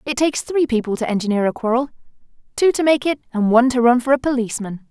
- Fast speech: Yes, fast, 220 wpm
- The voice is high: Yes, very high, 250 Hz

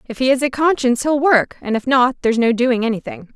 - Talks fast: Yes, fast, 250 wpm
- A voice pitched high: Yes, very high, 255 Hz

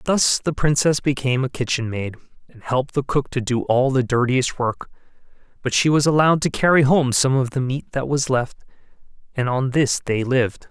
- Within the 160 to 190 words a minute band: No, average, 200 wpm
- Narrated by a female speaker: No, male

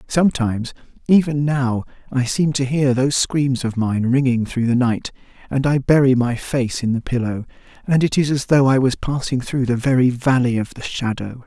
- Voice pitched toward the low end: Yes, low, 130 Hz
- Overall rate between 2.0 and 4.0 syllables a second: No, 5.0 syllables/s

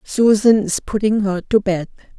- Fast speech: No, average, 165 wpm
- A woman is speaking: Yes, female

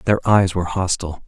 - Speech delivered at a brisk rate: No, average, 190 wpm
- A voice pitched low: Yes, very low, 95 Hz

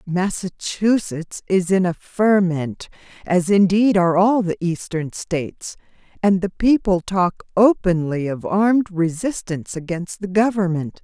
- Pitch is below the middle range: No, medium, 185 Hz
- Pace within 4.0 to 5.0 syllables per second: Yes, 4.2 syllables/s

